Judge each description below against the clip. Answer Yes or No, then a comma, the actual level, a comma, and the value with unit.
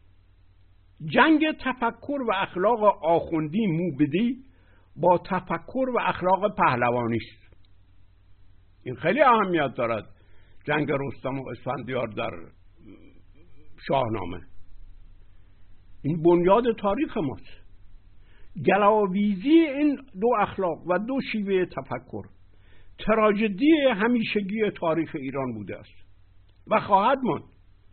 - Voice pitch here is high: No, low, 135 Hz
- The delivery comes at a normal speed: No, slow, 90 wpm